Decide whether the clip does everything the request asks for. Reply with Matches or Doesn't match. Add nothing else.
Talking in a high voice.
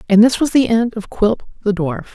Matches